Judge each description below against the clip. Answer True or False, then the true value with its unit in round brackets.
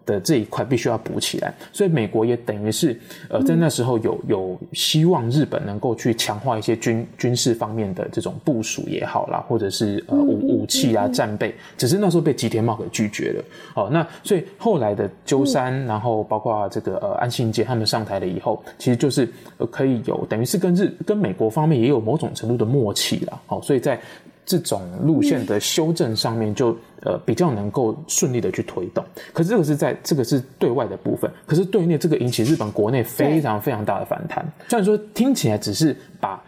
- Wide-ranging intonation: True (6.9 semitones)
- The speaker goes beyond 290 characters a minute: True (320 characters per minute)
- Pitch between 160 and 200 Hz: False (130 Hz)